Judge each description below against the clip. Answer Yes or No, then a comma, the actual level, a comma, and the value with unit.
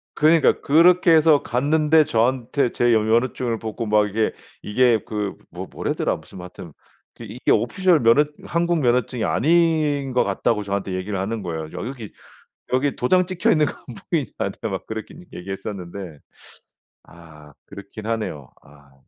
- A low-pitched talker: Yes, low, 115 Hz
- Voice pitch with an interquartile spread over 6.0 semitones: Yes, wide, 6.8 semitones